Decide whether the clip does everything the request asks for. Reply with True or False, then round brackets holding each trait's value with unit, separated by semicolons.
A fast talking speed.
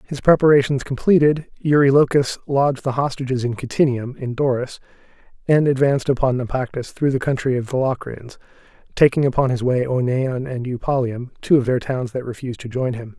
False (170 wpm)